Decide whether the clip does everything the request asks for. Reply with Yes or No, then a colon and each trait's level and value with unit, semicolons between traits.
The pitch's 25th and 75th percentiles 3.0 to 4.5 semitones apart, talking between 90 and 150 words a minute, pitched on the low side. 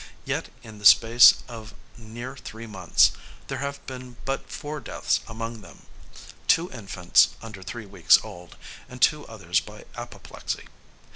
Yes: average, 3.4 semitones; average, 145 wpm; low, 115 Hz